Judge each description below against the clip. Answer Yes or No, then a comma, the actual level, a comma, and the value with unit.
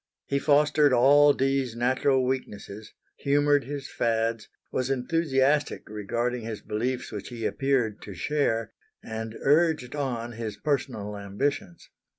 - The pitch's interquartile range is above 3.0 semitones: Yes, average, 4.1 semitones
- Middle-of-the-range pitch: No, low, 125 Hz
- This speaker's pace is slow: Yes, slow, 125 wpm